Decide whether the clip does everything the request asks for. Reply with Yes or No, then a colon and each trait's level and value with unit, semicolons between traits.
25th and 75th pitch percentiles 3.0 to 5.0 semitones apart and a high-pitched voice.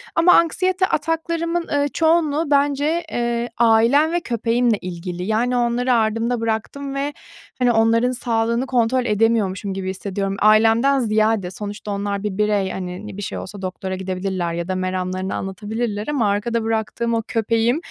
Yes: average, 4.2 semitones; high, 225 Hz